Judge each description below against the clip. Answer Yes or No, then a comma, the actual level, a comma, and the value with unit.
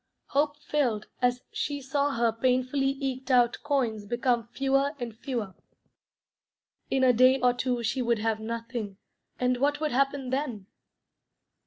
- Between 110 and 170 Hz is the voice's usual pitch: No, very high, 255 Hz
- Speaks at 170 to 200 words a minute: No, average, 145 wpm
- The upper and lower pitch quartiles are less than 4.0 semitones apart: Yes, average, 2.8 semitones